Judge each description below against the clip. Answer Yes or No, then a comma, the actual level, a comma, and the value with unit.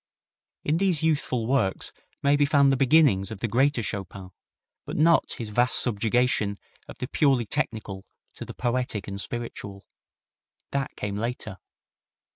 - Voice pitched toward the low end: Yes, low, 120 Hz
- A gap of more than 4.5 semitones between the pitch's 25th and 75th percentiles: Yes, average, 5.3 semitones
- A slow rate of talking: No, average, 145 wpm